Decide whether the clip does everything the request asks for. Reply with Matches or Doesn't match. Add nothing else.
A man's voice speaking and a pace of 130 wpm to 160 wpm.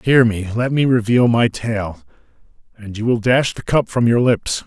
Doesn't match